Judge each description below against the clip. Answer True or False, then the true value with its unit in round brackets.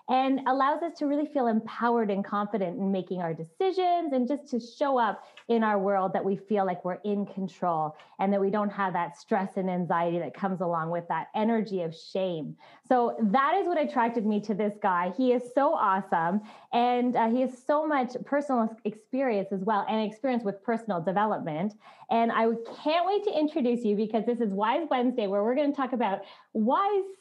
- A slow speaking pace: False (205 wpm)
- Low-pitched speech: False (220 Hz)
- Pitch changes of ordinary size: True (4.8 semitones)